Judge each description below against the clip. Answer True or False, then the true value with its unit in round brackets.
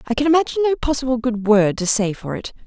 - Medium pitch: False (255 Hz)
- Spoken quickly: True (250 wpm)